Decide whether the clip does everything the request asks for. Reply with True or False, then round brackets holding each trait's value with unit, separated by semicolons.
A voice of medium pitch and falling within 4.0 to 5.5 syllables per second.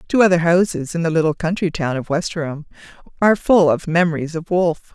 False (170 Hz; 6.1 syllables/s)